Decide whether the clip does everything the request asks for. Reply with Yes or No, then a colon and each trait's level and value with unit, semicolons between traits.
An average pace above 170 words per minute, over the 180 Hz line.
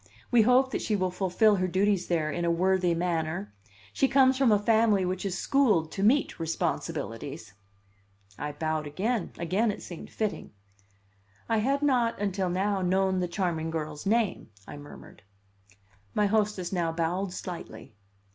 No: average, 155 wpm; high, 190 Hz